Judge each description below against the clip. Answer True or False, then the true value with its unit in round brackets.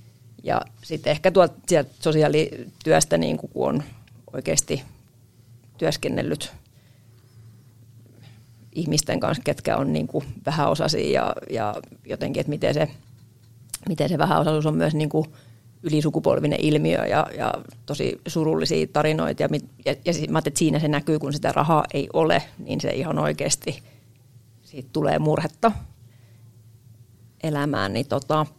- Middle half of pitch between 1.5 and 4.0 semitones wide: False (4.6 semitones)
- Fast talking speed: False (115 wpm)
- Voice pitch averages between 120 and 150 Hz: True (130 Hz)